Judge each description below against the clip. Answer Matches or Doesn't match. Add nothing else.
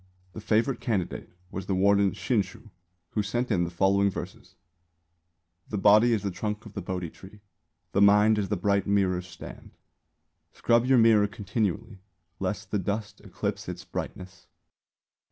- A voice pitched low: Matches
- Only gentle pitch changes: Matches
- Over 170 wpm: Doesn't match